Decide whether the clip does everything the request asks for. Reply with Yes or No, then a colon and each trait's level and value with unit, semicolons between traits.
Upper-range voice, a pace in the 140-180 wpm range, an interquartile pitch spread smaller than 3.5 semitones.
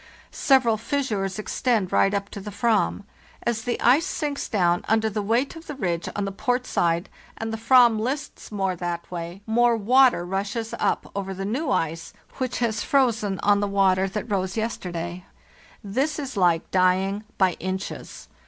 No: high, 205 Hz; average, 170 wpm; average, 4.2 semitones